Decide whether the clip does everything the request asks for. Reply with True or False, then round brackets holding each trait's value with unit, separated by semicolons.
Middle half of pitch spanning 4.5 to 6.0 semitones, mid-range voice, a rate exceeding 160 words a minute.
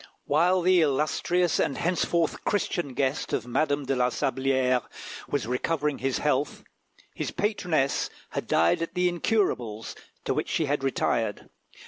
False (4.9 semitones; 145 Hz; 140 wpm)